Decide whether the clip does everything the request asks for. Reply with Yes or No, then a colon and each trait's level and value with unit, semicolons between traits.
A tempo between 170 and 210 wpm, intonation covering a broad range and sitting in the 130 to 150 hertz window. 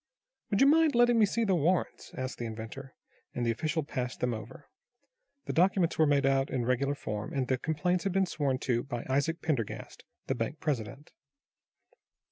Yes: average, 185 wpm; wide, 6.1 semitones; medium, 140 Hz